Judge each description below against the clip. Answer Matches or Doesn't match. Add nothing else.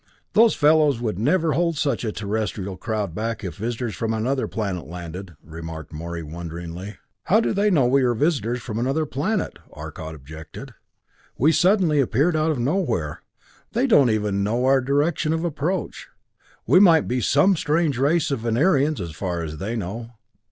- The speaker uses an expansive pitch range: Matches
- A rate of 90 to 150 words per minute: Doesn't match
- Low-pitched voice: Matches